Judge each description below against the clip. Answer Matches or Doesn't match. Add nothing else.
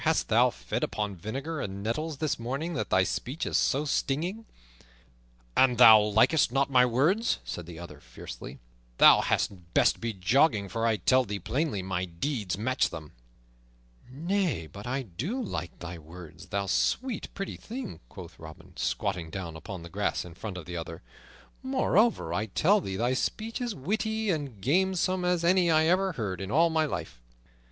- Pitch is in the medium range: Doesn't match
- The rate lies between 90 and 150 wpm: Doesn't match